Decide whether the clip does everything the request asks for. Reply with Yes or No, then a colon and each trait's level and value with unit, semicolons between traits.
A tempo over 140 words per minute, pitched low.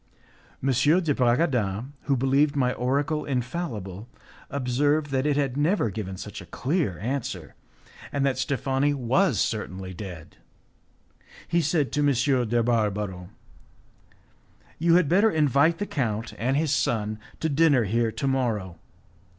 No: slow, 135 wpm; low, 130 Hz